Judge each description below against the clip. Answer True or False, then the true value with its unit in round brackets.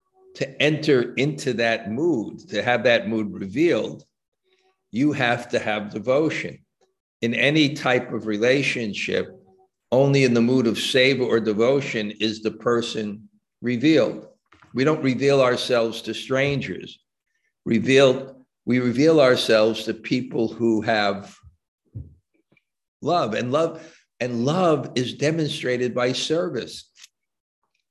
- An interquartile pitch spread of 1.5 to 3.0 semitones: False (4.0 semitones)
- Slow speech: True (120 wpm)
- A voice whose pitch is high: False (125 Hz)